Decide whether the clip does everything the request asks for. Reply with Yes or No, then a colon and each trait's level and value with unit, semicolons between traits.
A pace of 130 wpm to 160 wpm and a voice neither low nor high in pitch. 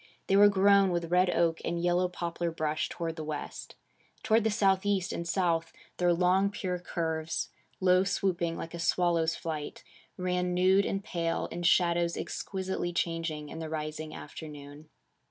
Yes: average, 155 wpm; medium, 175 Hz